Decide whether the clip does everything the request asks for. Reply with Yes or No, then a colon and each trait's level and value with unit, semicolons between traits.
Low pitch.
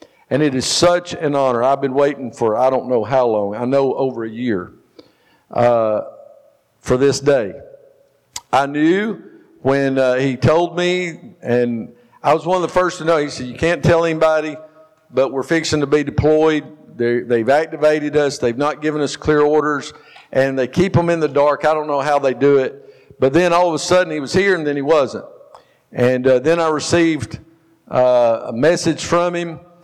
No: medium, 150 Hz